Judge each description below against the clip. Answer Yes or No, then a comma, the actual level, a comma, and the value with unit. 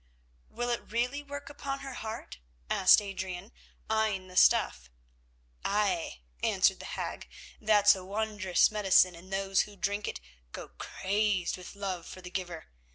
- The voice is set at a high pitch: Yes, high, 200 Hz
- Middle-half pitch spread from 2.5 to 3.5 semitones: Yes, average, 2.8 semitones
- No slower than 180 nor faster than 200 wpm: No, average, 150 wpm